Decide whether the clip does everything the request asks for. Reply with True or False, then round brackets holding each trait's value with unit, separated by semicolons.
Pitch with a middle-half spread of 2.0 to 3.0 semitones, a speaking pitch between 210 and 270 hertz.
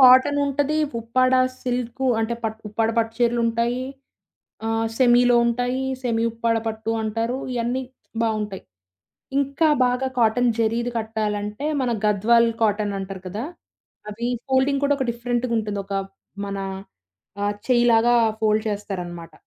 True (2.4 semitones; 230 Hz)